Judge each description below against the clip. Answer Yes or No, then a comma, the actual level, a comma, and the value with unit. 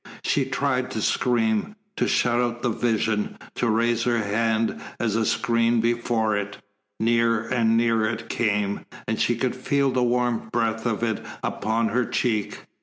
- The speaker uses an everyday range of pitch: No, narrow, 1.5 semitones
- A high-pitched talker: No, low, 115 Hz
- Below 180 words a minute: Yes, average, 165 wpm